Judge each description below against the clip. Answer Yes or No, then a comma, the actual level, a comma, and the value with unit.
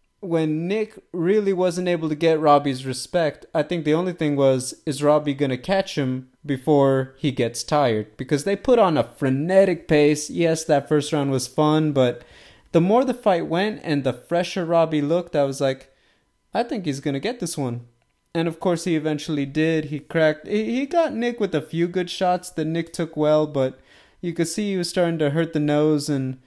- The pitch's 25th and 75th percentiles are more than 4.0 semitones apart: No, average, 3.6 semitones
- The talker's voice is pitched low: No, medium, 155 Hz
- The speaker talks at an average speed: No, fast, 210 wpm